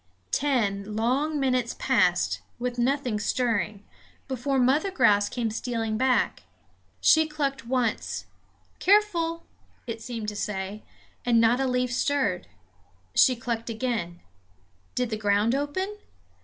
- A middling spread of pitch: Yes, average, 3.8 semitones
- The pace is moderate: No, slow, 120 wpm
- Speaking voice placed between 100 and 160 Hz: No, high, 245 Hz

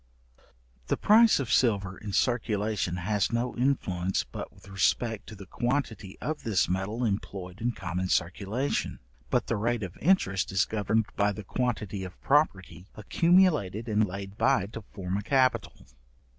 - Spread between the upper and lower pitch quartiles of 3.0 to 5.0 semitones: Yes, average, 4.0 semitones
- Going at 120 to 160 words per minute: Yes, average, 155 wpm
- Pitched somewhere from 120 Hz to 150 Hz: No, low, 105 Hz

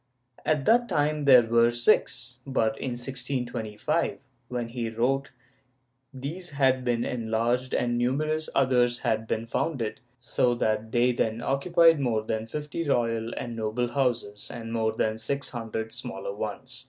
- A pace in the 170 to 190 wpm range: No, average, 145 wpm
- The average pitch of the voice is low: Yes, low, 120 Hz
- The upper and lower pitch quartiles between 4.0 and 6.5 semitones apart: No, average, 3.2 semitones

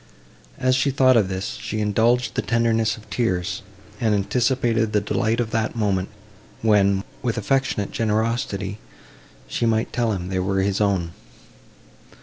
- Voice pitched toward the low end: Yes, low, 110 Hz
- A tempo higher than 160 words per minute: No, average, 145 wpm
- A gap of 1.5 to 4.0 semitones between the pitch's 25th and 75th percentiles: Yes, average, 2.9 semitones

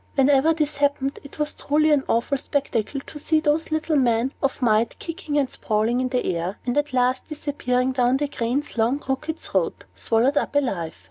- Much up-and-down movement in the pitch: No, average, 3.2 semitones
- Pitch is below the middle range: No, very high, 270 Hz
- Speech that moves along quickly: No, average, 190 wpm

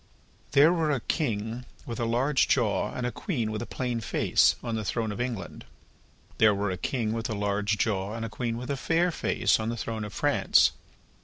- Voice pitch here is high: No, low, 115 Hz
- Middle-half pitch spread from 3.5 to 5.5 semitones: No, average, 2.9 semitones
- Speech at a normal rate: No, fast, 215 wpm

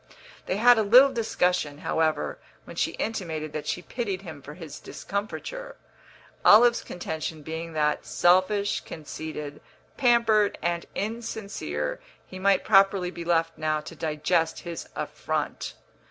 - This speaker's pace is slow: Yes, slow, 130 wpm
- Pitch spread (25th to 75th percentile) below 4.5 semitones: No, average, 5.1 semitones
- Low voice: No, medium, 180 Hz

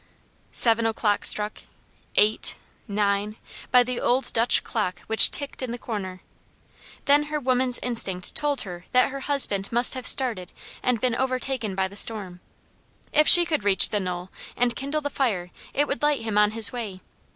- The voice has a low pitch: No, high, 230 Hz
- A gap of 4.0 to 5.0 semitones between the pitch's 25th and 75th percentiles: Yes, average, 4.4 semitones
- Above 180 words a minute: No, average, 175 wpm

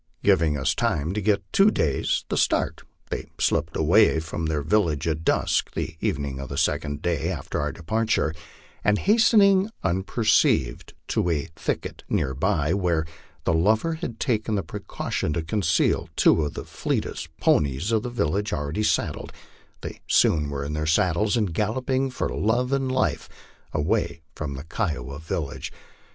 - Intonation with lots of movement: Yes, wide, 6.4 semitones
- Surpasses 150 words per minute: Yes, average, 160 wpm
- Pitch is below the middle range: Yes, very low, 85 Hz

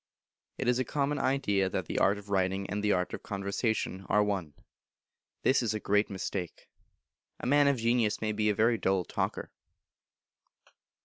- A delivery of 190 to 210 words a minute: No, average, 175 wpm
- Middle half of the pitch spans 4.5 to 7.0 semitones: No, average, 3.6 semitones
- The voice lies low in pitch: Yes, low, 105 Hz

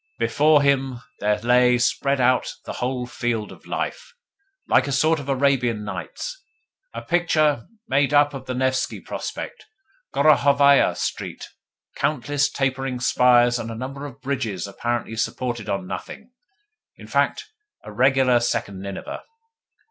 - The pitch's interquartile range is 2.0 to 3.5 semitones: Yes, average, 2.8 semitones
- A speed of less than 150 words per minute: Yes, slow, 135 wpm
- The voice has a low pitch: Yes, low, 130 Hz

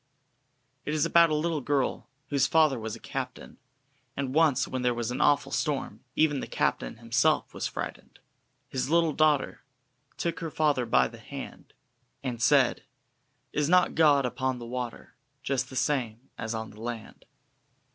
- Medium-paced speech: Yes, average, 170 wpm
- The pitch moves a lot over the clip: No, average, 3.9 semitones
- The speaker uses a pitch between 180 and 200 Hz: No, low, 135 Hz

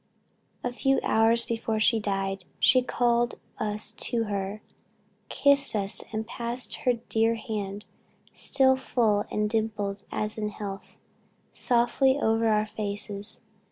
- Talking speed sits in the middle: No, slow, 125 wpm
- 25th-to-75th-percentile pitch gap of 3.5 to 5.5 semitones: No, narrow, 2.4 semitones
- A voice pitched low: No, high, 220 Hz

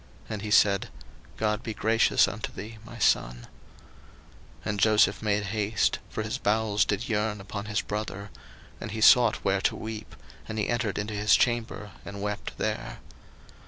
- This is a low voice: Yes, low, 105 Hz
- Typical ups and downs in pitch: No, narrow, 1.4 semitones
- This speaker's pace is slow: No, average, 165 wpm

